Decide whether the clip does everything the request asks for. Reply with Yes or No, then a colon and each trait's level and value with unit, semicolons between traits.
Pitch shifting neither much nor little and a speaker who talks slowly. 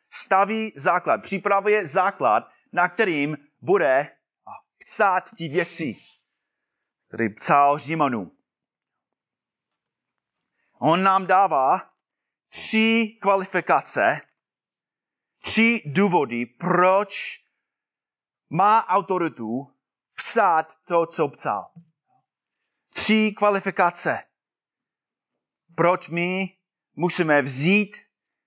Yes: average, 4.1 semitones; slow, 70 wpm